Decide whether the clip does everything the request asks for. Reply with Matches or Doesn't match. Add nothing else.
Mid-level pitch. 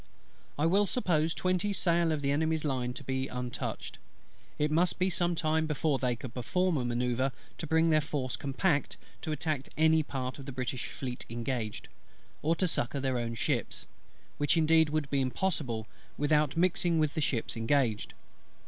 Matches